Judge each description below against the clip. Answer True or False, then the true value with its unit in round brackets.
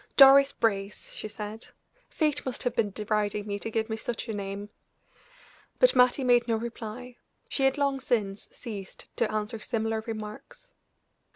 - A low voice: False (225 Hz)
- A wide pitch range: False (3.0 semitones)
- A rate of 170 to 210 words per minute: False (160 wpm)